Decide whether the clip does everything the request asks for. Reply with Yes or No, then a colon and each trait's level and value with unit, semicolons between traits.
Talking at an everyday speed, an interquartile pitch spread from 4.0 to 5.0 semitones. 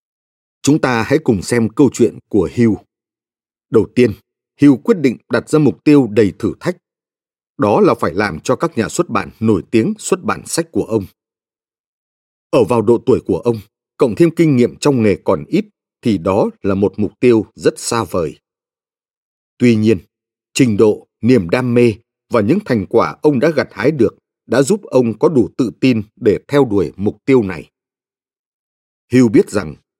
Yes: average, 185 wpm; average, 4.3 semitones